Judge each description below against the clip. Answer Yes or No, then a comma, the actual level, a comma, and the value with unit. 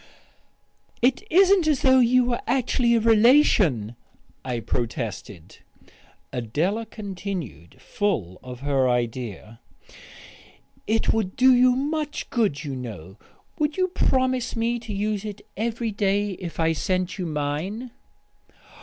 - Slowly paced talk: Yes, slow, 125 wpm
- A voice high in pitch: Yes, high, 205 Hz